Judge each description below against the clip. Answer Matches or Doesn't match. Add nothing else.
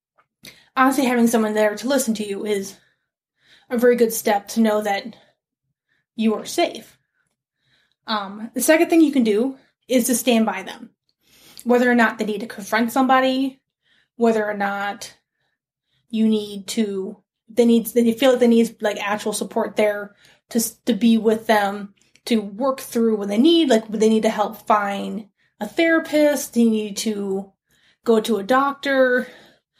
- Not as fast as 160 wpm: Doesn't match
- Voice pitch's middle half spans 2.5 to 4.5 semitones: Matches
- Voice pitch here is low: Doesn't match